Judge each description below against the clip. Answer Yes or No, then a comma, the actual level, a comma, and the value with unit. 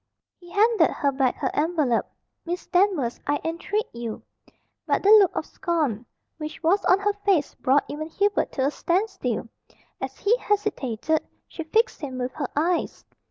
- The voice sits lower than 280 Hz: No, very high, 325 Hz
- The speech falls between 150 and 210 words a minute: Yes, average, 165 wpm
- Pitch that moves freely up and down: Yes, wide, 6.4 semitones